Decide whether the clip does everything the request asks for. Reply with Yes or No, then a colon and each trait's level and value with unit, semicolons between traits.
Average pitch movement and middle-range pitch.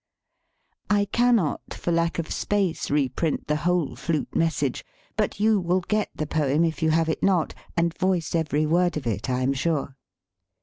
Yes: average, 3.1 semitones; medium, 165 Hz